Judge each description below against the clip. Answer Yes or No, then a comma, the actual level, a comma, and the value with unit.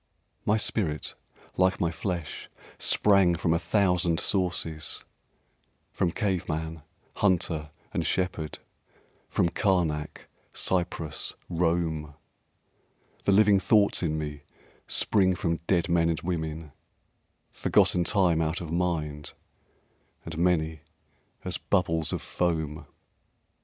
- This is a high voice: No, very low, 85 Hz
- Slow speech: Yes, slow, 105 wpm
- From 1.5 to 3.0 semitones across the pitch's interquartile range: Yes, narrow, 2.6 semitones